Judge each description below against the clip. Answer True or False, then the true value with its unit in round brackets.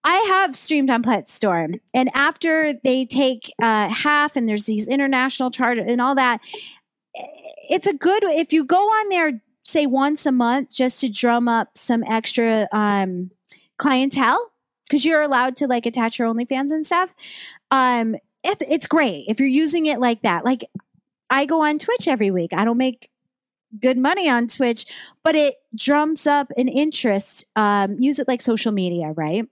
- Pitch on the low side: False (255 Hz)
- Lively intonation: False (4.6 semitones)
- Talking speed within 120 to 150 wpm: False (175 wpm)